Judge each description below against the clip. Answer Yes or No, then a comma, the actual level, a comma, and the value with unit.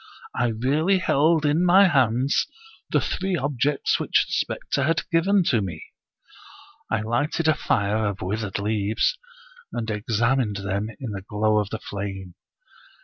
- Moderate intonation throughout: No, wide, 6.5 semitones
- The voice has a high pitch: No, low, 115 Hz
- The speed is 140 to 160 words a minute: Yes, average, 150 wpm